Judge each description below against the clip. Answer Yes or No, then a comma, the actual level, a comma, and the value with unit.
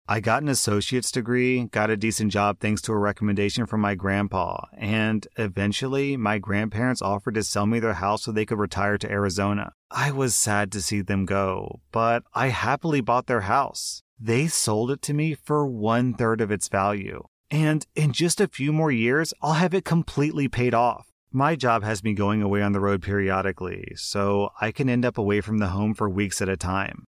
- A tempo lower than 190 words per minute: No, fast, 205 wpm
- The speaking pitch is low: Yes, low, 110 Hz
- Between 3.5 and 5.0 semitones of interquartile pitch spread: Yes, average, 3.9 semitones